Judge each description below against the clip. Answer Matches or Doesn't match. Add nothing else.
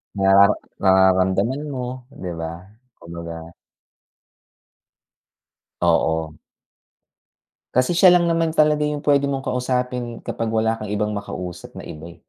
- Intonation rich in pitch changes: Matches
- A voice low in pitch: Matches